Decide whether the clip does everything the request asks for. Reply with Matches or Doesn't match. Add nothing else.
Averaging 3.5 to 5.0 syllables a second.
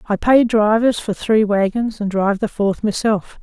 Matches